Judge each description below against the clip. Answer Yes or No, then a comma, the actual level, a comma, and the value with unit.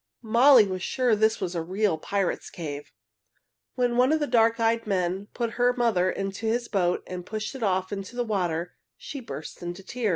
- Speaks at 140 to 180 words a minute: No, average, 195 wpm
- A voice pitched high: Yes, high, 215 Hz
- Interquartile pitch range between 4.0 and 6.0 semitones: Yes, average, 4.4 semitones